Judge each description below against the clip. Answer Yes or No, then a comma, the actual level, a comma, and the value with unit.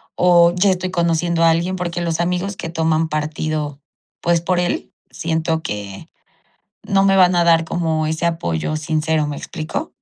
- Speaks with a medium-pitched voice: Yes, medium, 165 Hz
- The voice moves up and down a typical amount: No, narrow, 1.9 semitones